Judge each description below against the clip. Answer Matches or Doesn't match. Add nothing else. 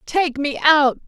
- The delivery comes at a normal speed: Matches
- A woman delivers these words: Matches